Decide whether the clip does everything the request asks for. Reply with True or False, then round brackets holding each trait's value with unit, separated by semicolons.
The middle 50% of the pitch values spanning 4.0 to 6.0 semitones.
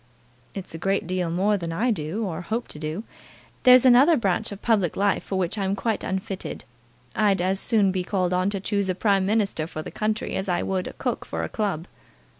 False (2.7 semitones)